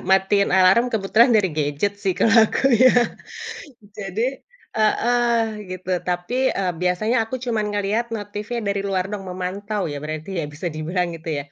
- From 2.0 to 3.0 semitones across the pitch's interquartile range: No, average, 3.7 semitones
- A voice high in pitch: Yes, high, 200 Hz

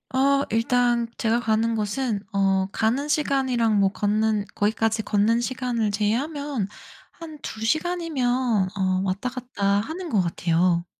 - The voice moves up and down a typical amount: Yes, average, 4.2 semitones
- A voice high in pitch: Yes, high, 230 Hz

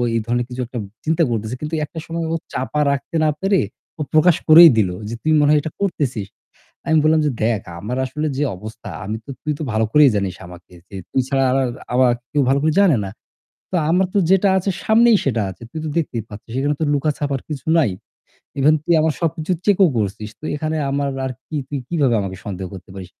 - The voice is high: No, medium, 145 Hz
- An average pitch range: No, wide, 5.8 semitones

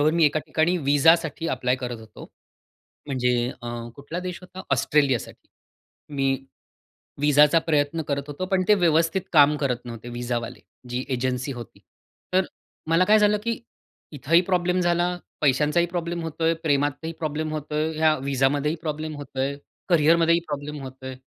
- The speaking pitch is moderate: Yes, medium, 150 Hz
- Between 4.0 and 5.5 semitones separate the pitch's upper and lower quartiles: No, average, 3.5 semitones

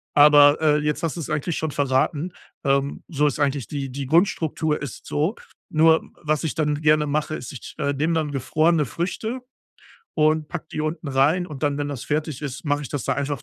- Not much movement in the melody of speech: Yes, narrow, 1.8 semitones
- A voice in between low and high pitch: Yes, medium, 150 Hz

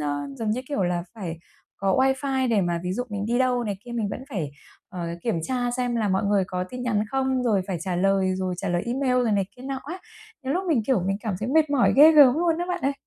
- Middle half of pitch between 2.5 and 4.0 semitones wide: No, wide, 5.6 semitones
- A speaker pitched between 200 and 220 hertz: No, high, 230 Hz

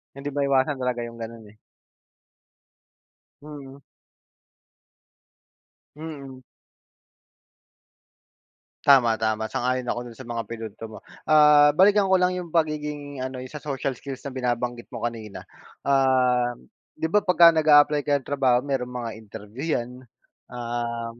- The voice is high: No, low, 130 Hz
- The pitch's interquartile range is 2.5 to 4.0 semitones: Yes, average, 3.7 semitones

